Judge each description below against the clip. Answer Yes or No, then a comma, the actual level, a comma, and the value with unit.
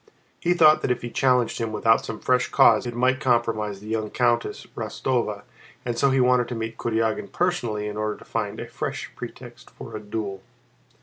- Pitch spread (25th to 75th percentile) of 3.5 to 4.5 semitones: No, average, 2.8 semitones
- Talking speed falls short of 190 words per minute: No, average, 195 wpm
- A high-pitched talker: No, low, 115 Hz